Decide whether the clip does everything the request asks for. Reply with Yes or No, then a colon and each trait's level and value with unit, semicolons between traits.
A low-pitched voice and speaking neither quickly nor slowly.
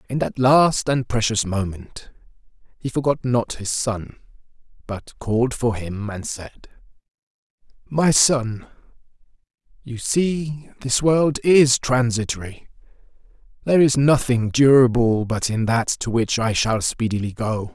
No: low, 120 Hz; slow, 130 wpm